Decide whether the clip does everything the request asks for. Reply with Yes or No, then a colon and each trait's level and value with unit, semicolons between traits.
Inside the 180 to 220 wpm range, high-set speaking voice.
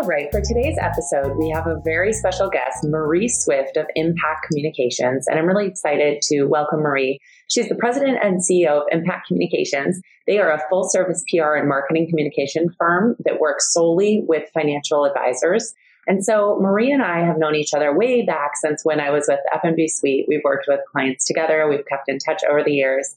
No: average, 195 wpm; medium, 155 Hz